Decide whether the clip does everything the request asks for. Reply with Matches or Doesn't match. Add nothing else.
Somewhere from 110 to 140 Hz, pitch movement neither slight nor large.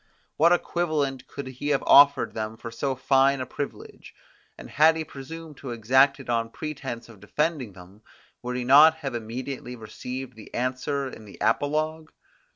Matches